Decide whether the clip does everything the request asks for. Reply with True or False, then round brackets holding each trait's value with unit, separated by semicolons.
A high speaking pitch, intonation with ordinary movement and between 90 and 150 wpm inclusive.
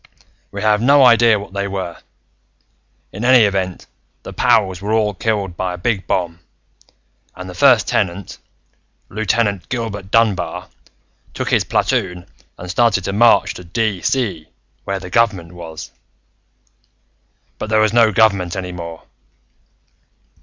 False (100 Hz; 3.6 semitones; 135 wpm)